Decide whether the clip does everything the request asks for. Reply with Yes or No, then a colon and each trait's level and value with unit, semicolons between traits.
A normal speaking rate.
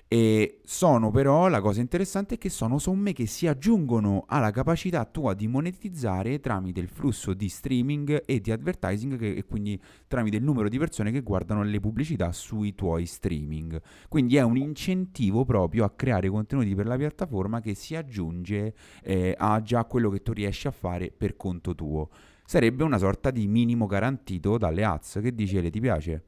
No: fast, 185 wpm